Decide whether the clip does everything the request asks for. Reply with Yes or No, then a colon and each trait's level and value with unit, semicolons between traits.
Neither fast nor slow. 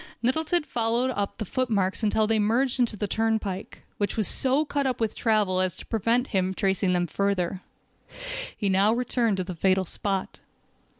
Yes: average, 175 wpm